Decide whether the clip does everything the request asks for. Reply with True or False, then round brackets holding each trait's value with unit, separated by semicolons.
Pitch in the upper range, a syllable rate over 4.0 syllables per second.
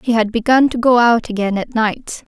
True (230 Hz; 5.1 syllables/s)